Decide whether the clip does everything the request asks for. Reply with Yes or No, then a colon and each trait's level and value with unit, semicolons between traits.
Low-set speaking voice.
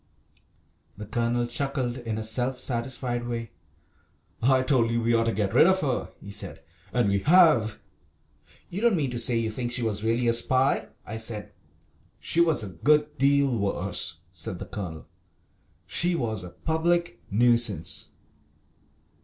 Yes: low, 120 Hz